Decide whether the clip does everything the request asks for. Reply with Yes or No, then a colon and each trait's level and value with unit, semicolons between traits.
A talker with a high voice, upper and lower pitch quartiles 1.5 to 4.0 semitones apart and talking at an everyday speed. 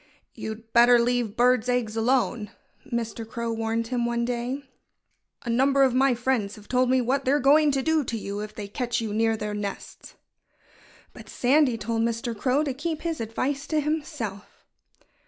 Yes: high, 240 Hz; average, 3.0 semitones; average, 175 wpm